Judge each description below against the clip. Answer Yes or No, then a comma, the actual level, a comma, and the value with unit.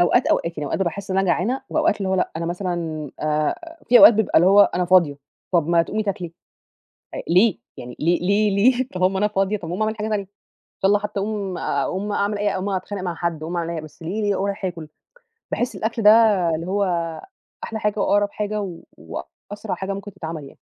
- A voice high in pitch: Yes, high, 195 Hz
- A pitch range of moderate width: Yes, average, 3.4 semitones